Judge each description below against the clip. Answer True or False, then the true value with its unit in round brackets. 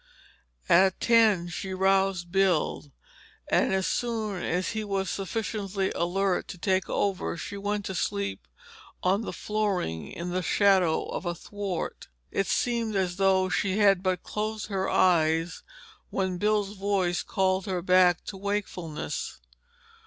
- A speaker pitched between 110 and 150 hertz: False (190 Hz)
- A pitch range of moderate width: False (2.2 semitones)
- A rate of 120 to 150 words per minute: True (140 wpm)